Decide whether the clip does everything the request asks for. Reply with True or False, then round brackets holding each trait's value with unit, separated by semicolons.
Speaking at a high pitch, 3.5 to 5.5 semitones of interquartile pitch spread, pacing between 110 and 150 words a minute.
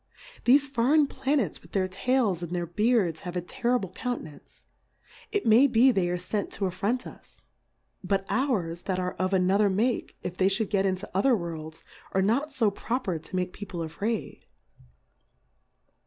False (195 Hz; 5.2 semitones; 170 wpm)